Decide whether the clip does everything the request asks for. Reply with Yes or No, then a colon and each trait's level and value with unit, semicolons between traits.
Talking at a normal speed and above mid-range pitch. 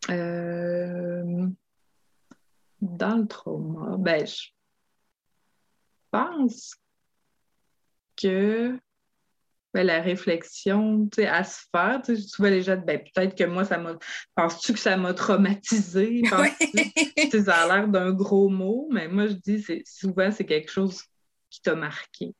No: slow, 135 wpm; high, 195 Hz